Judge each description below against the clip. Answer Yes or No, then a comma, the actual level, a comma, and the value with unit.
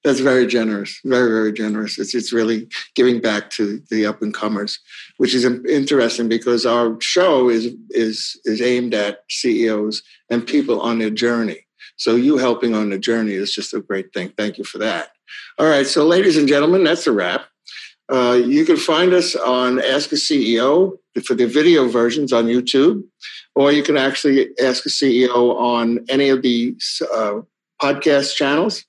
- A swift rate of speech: No, average, 180 wpm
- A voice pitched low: Yes, low, 120 Hz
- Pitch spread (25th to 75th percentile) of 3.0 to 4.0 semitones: Yes, average, 3.7 semitones